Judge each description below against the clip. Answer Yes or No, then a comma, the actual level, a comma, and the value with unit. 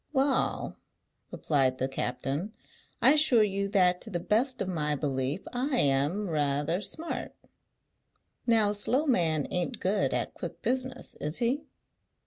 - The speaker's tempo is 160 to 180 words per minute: No, average, 140 wpm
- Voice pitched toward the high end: Yes, high, 195 Hz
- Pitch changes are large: Yes, wide, 8.6 semitones